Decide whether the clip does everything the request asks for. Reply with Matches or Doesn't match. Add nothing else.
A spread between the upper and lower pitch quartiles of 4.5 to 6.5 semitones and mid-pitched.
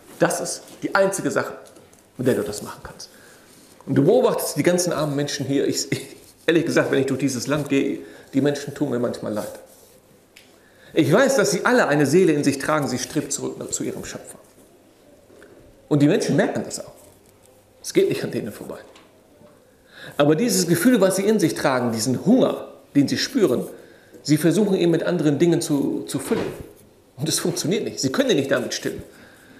Matches